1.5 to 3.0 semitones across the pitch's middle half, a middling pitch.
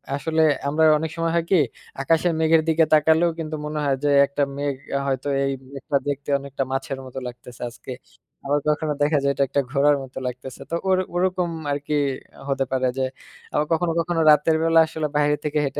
Yes: average, 2.7 semitones; medium, 150 Hz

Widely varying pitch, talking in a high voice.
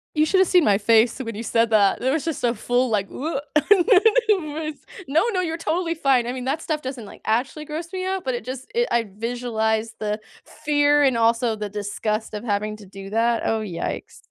Yes: wide, 5.9 semitones; high, 245 Hz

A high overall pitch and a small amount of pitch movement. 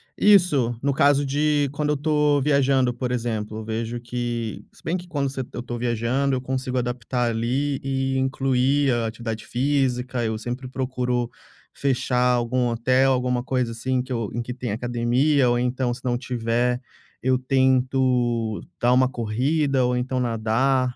No: low, 125 Hz; narrow, 1.9 semitones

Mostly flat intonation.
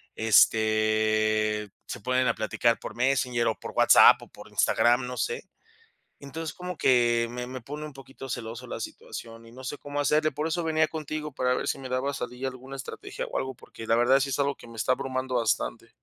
No: average, 3.3 semitones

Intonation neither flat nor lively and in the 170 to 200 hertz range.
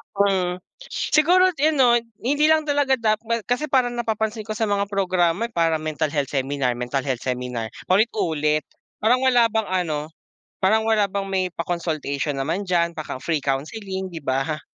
No: wide, 6.7 semitones; medium, 185 Hz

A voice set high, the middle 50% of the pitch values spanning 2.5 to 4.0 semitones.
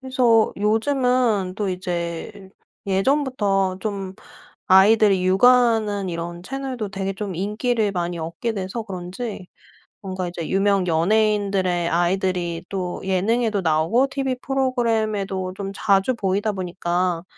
Yes: high, 195 Hz; average, 3.4 semitones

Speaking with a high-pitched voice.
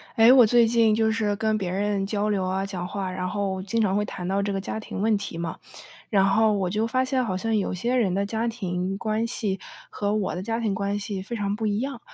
Yes: high, 205 Hz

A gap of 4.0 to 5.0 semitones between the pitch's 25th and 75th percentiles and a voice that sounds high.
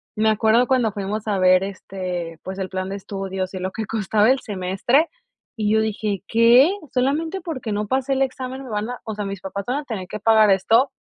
Yes: average, 4.4 semitones; high, 215 Hz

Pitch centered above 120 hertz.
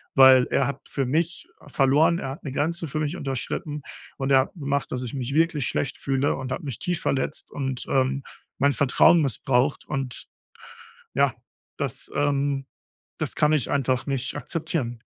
Yes: medium, 140 Hz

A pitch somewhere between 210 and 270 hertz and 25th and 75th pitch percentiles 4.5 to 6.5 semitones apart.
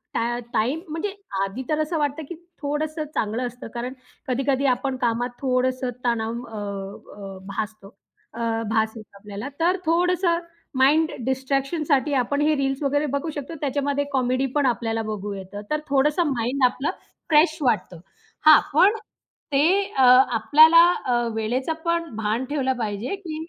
Yes: very high, 265 Hz; average, 4.8 semitones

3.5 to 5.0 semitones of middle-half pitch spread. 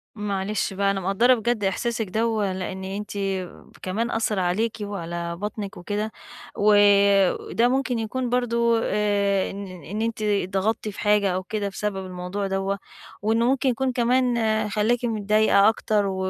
No: average, 2.7 semitones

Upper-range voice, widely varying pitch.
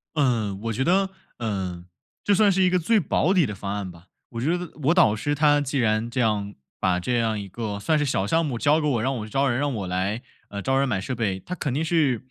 No: low, 125 Hz; wide, 6.5 semitones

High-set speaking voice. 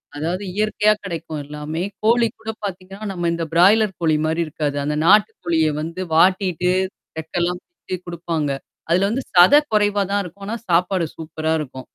No: medium, 175 Hz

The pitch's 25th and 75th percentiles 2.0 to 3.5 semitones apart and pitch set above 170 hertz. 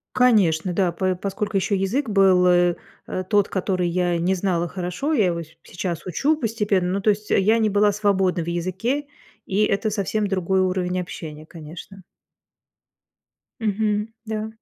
Yes: average, 2.8 semitones; high, 190 Hz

